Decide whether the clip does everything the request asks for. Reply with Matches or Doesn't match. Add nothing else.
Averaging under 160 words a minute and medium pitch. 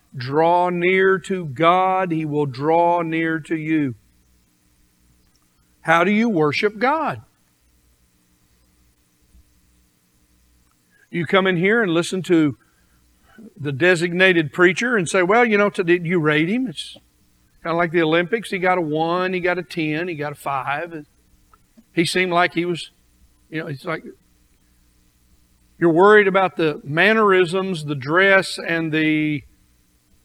Matches